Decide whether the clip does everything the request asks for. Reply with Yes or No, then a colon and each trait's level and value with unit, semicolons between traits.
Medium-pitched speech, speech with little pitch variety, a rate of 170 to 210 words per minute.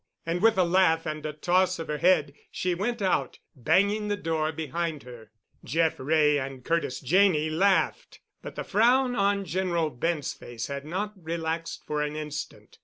No: medium, 165 Hz; average, 3.9 semitones; average, 175 wpm